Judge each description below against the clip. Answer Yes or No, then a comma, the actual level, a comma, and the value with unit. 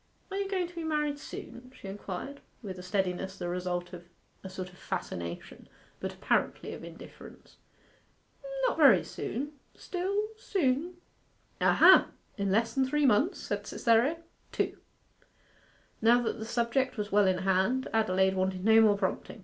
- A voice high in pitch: Yes, high, 220 Hz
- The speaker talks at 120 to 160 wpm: Yes, average, 155 wpm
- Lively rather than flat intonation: Yes, wide, 7.0 semitones